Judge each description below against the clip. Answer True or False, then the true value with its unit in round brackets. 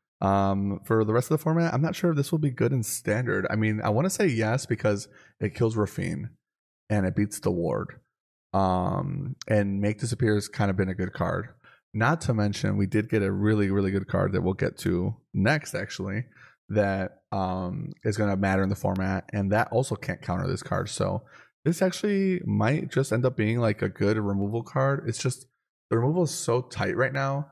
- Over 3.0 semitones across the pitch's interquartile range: True (5.4 semitones)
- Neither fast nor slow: False (215 wpm)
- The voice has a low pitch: True (110 Hz)